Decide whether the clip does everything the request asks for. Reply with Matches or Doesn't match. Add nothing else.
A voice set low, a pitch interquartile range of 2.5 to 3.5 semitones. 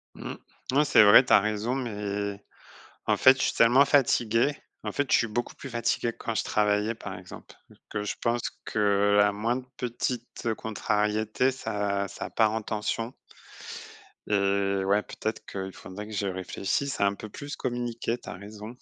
Matches